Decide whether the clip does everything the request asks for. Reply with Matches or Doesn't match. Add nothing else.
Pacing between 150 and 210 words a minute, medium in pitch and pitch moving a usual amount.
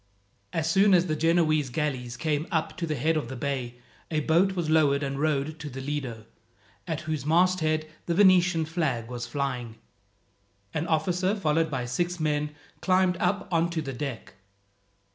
Matches